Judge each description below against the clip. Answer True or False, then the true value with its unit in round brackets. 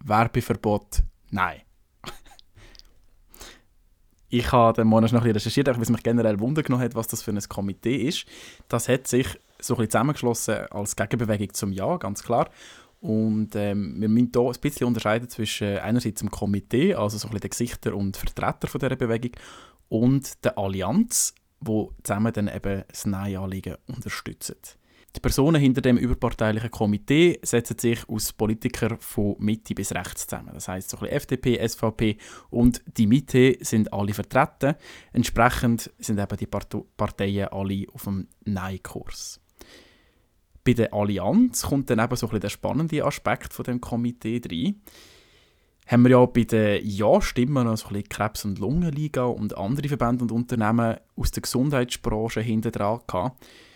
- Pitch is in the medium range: False (115 Hz)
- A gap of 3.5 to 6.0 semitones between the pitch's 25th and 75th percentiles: False (3.1 semitones)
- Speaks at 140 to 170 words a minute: True (160 wpm)